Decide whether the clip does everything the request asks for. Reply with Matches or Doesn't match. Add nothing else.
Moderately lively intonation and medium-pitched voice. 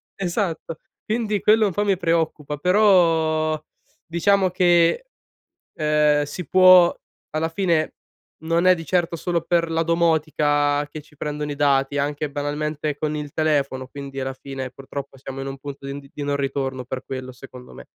Matches